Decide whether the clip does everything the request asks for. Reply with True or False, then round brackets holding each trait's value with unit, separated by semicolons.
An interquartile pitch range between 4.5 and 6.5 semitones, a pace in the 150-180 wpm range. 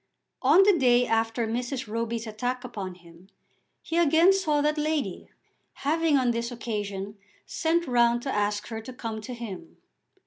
True (5.0 semitones; 160 wpm)